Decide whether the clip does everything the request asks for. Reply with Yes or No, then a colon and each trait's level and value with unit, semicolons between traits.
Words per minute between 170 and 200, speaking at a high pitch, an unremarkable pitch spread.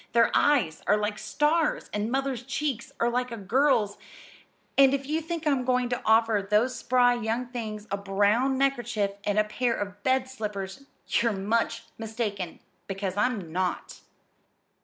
No: average, 160 wpm; high, 230 Hz; average, 3.9 semitones